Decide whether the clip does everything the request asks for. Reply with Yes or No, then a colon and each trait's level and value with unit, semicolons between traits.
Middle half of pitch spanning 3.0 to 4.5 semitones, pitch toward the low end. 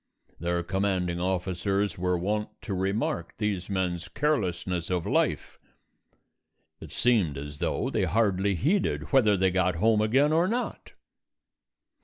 Yes: average, 3.3 semitones; very low, 95 Hz